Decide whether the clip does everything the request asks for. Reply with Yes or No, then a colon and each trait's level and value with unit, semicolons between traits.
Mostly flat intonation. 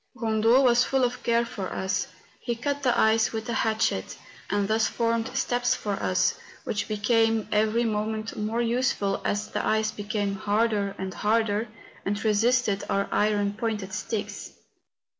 Yes: narrow, 2.1 semitones